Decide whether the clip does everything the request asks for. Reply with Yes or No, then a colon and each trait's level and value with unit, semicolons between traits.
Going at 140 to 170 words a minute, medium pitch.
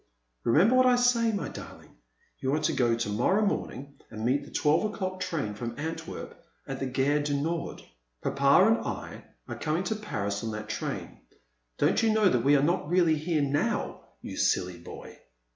No: average, 190 wpm; medium, 150 Hz